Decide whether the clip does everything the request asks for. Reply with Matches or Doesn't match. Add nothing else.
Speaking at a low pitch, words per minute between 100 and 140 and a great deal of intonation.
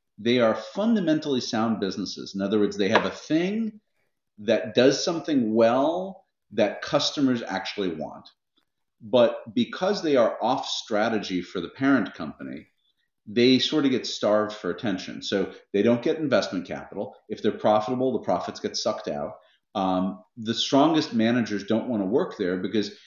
Doesn't match